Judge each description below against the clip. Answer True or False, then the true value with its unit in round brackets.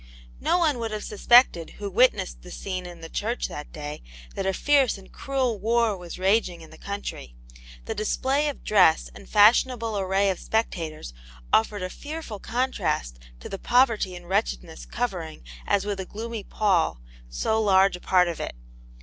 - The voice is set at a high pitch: True (200 Hz)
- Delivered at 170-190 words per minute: True (175 wpm)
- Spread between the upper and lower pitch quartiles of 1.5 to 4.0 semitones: False (4.6 semitones)